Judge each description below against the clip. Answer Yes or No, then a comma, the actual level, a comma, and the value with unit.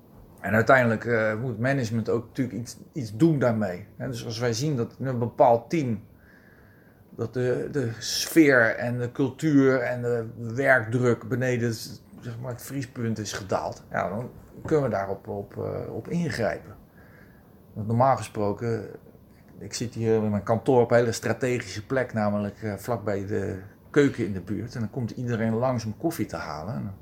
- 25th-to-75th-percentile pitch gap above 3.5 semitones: No, average, 2.8 semitones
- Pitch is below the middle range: Yes, low, 115 Hz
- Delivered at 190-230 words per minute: No, average, 170 wpm